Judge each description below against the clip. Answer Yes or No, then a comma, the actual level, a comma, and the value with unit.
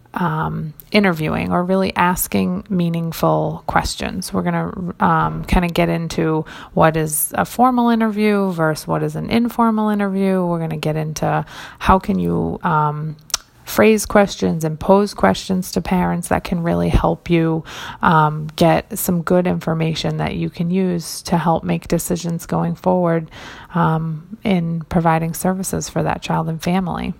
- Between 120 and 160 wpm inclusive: Yes, average, 155 wpm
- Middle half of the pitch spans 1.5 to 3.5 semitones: Yes, average, 3.1 semitones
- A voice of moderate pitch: Yes, medium, 170 Hz